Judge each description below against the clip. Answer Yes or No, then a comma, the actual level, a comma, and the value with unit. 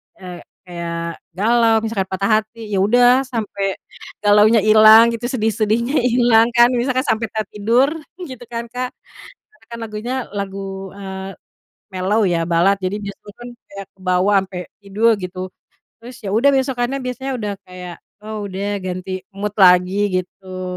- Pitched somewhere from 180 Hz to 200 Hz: No, high, 210 Hz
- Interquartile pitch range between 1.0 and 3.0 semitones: No, average, 3.6 semitones